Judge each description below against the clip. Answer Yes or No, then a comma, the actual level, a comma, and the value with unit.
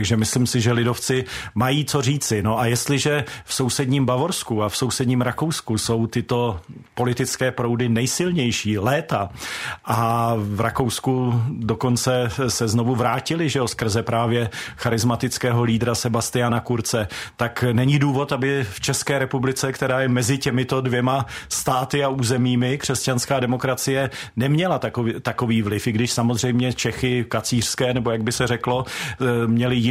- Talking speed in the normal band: Yes, average, 140 wpm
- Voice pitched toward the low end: Yes, low, 125 Hz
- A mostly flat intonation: Yes, narrow, 2.2 semitones